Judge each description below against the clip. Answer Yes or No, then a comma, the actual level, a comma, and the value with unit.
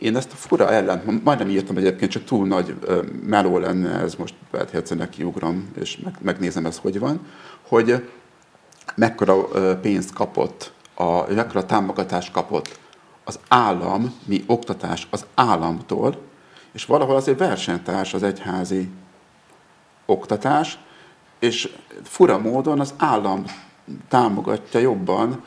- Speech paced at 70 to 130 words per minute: Yes, average, 125 wpm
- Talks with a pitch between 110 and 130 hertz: No, low, 100 Hz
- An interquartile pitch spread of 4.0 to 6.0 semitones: Yes, average, 4.7 semitones